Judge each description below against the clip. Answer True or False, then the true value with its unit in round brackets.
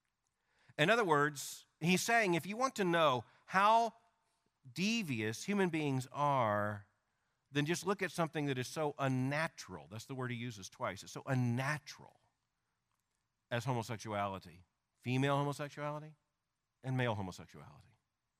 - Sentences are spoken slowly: True (130 wpm)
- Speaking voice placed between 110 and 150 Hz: True (135 Hz)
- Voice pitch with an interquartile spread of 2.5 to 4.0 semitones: False (4.6 semitones)